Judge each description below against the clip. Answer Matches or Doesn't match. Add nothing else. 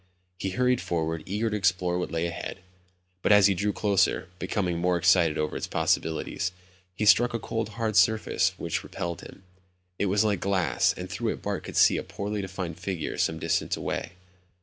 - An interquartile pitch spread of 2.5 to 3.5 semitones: Matches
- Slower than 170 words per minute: Doesn't match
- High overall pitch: Doesn't match